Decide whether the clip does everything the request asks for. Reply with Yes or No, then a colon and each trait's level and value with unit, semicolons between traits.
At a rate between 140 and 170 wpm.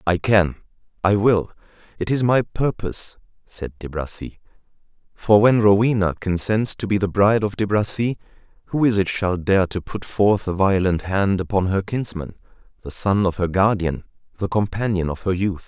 Yes: average, 160 wpm